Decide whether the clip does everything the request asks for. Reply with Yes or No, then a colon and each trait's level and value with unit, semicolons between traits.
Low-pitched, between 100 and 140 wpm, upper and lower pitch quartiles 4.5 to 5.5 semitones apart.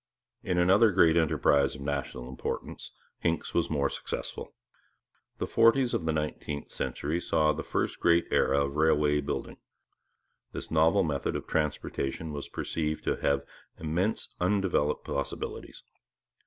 No: very low, 80 Hz; slow, 135 wpm; average, 3.1 semitones